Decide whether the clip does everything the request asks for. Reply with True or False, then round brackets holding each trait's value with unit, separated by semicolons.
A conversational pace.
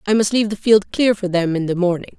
False (300 wpm)